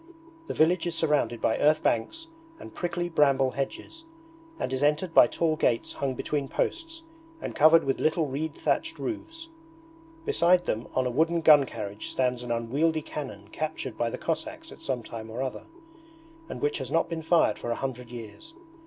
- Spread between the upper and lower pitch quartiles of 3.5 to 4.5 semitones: No, average, 4.9 semitones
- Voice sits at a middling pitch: Yes, medium, 150 Hz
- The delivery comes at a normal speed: Yes, average, 180 wpm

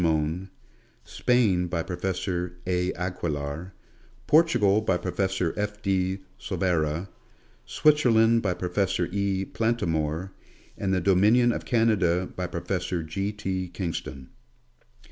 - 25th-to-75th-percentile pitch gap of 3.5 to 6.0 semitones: No, average, 2.7 semitones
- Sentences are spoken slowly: Yes, slow, 105 wpm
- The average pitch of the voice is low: Yes, very low, 95 Hz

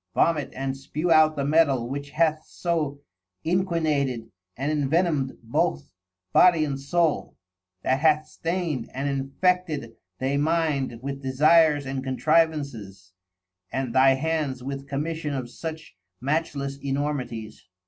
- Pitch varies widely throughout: No, average, 3.1 semitones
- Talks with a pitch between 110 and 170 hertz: Yes, medium, 140 Hz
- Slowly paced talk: Yes, slow, 120 wpm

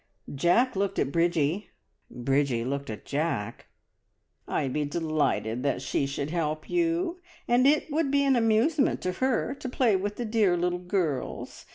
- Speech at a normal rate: Yes, average, 160 wpm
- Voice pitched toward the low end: No, medium, 180 Hz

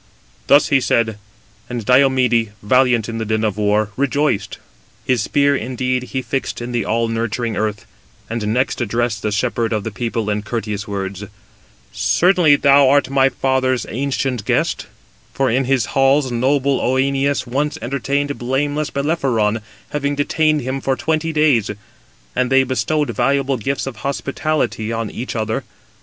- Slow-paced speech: No, average, 150 wpm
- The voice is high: No, low, 130 Hz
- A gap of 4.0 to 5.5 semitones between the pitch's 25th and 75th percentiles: No, average, 3.6 semitones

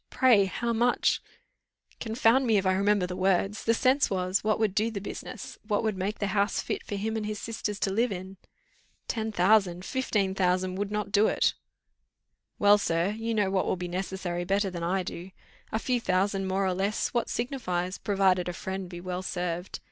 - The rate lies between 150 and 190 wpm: No, average, 200 wpm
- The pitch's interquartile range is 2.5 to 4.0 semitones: Yes, average, 2.9 semitones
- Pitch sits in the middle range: No, high, 195 Hz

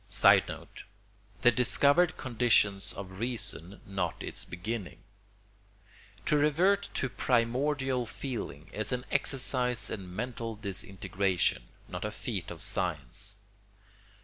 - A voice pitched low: Yes, low, 115 Hz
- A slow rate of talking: Yes, slow, 105 wpm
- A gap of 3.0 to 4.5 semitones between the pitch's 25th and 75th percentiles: No, average, 5.0 semitones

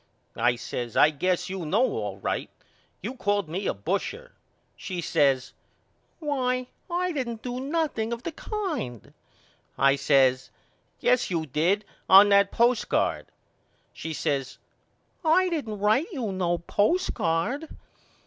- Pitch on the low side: No, high, 205 Hz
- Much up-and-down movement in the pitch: Yes, wide, 8.7 semitones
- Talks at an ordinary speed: No, slow, 130 wpm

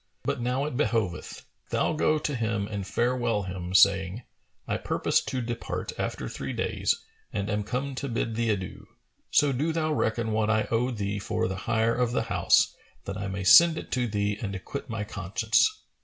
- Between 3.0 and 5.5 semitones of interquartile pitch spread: Yes, average, 3.9 semitones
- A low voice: Yes, low, 115 Hz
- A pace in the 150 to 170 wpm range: No, average, 190 wpm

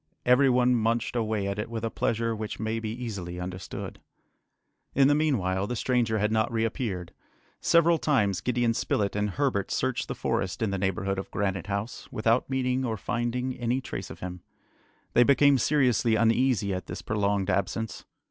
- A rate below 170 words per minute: No, average, 175 wpm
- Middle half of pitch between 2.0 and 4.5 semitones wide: Yes, average, 3.8 semitones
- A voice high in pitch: No, low, 115 Hz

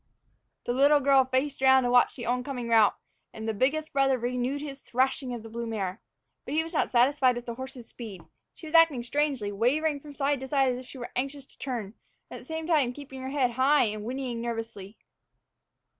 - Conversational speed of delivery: No, fast, 215 wpm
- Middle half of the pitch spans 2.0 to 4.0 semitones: Yes, average, 2.9 semitones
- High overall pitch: Yes, very high, 260 Hz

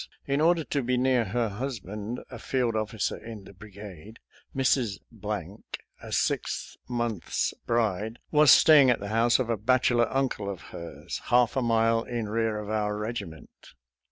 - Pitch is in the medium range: No, low, 115 Hz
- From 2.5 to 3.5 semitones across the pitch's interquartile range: Yes, average, 3.0 semitones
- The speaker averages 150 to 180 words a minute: Yes, average, 165 wpm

